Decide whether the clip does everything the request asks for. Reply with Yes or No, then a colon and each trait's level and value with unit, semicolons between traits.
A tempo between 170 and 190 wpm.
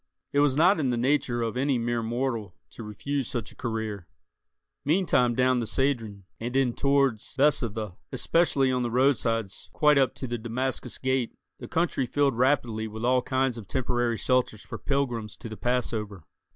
Yes: average, 175 wpm